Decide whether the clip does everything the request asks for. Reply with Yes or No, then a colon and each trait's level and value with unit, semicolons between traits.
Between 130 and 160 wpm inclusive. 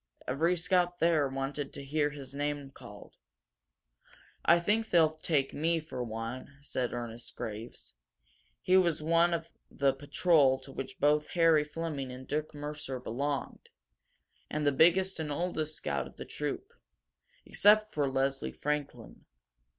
Yes: average, 145 wpm